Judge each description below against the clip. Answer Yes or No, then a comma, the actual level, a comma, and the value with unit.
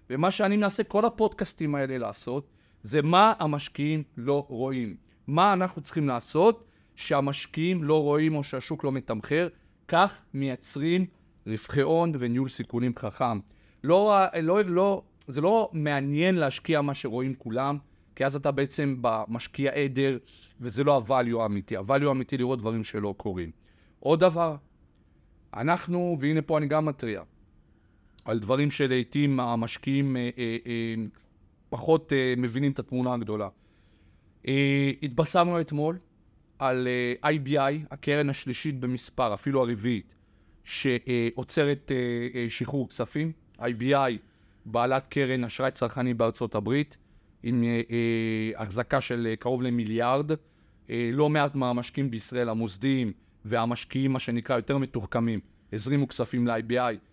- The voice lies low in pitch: Yes, low, 130 Hz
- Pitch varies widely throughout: No, average, 3.9 semitones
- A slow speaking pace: No, average, 125 wpm